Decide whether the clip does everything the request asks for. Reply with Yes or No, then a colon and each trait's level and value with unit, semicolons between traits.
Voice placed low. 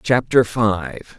Yes: low, 105 Hz